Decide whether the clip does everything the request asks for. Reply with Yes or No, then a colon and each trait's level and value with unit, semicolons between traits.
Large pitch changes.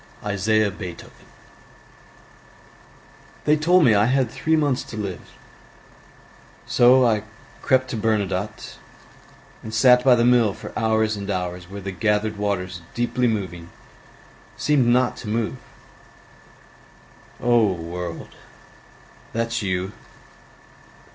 No: average, 3.9 semitones